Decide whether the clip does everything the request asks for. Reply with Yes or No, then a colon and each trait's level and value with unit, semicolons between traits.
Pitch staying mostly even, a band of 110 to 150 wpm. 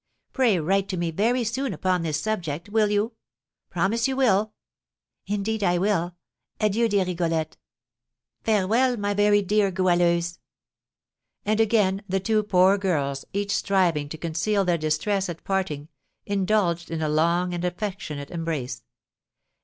No: average, 3.6 semitones; average, 140 wpm